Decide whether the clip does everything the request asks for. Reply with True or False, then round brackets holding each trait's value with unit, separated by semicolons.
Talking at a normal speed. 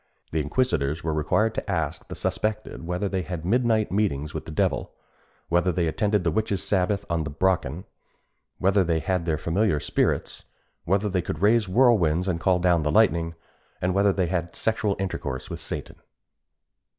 True (175 wpm)